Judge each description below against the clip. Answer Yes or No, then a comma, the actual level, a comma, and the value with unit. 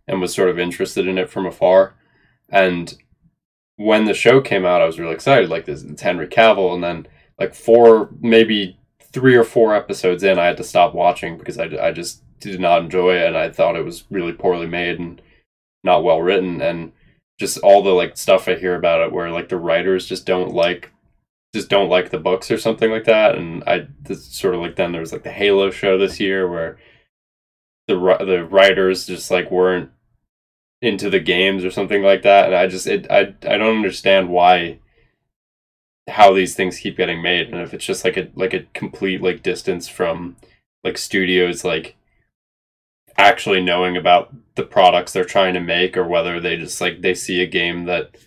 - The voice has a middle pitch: No, very low, 90 Hz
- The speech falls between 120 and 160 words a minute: No, average, 200 wpm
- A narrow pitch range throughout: Yes, narrow, 2.3 semitones